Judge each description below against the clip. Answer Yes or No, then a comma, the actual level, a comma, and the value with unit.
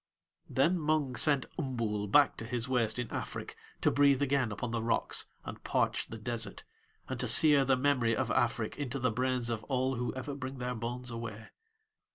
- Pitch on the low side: Yes, low, 125 Hz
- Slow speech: No, average, 190 wpm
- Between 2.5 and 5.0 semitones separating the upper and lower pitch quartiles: Yes, average, 2.9 semitones